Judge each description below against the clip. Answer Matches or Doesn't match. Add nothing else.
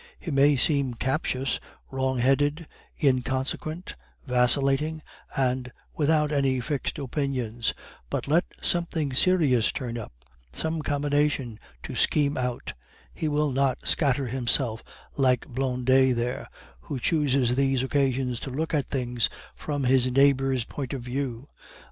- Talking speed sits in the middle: Doesn't match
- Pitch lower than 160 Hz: Matches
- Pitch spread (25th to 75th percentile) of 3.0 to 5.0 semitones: Doesn't match